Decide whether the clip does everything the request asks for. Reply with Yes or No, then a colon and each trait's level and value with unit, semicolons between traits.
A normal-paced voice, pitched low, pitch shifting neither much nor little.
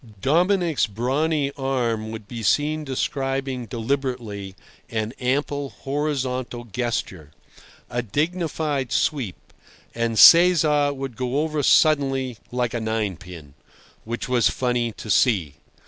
No: slow, 105 wpm; low, 125 Hz; average, 4.1 semitones